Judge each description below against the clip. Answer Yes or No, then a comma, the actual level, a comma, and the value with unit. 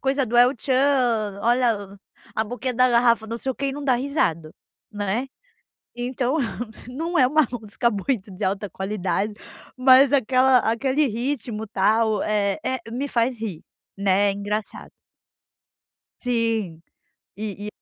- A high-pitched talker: Yes, high, 235 Hz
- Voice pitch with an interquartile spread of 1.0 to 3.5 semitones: No, average, 3.9 semitones